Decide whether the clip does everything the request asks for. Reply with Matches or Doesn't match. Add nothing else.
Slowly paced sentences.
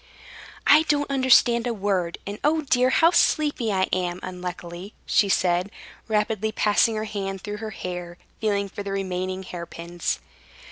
Doesn't match